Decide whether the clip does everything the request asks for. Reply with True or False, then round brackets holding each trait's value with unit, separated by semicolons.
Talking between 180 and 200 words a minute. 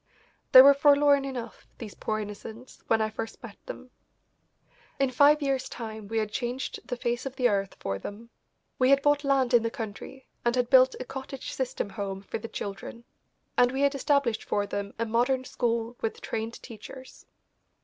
True (185 wpm)